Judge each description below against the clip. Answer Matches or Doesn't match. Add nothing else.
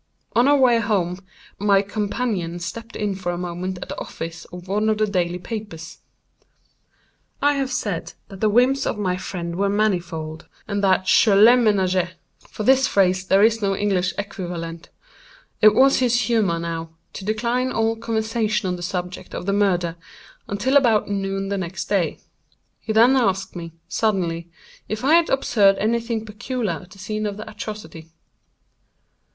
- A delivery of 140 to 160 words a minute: Doesn't match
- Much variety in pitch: Doesn't match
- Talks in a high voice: Matches